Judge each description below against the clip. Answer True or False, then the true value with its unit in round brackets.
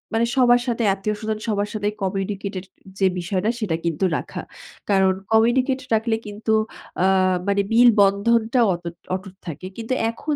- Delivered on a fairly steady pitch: False (3.1 semitones)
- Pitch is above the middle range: True (210 Hz)